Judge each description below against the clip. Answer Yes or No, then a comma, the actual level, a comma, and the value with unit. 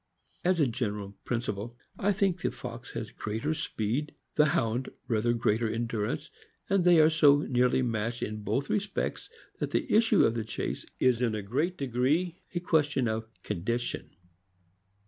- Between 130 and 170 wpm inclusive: Yes, average, 165 wpm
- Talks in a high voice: No, low, 125 Hz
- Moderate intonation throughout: No, wide, 5.8 semitones